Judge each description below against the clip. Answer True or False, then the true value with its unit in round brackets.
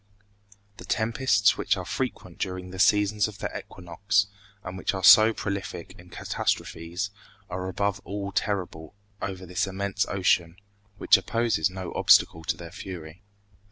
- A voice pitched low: True (95 Hz)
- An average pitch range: False (2.1 semitones)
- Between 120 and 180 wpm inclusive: True (145 wpm)